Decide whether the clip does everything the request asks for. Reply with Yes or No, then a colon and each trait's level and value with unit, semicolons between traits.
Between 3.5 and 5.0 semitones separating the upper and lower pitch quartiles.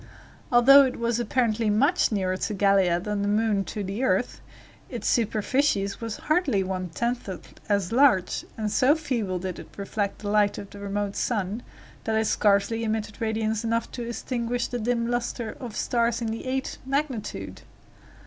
No: average, 3.1 semitones